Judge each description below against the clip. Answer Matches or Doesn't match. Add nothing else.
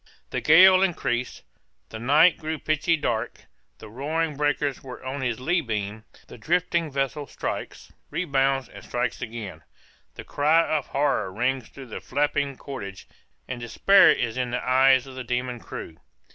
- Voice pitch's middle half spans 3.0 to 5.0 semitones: Matches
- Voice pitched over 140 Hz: Doesn't match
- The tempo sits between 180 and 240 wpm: Doesn't match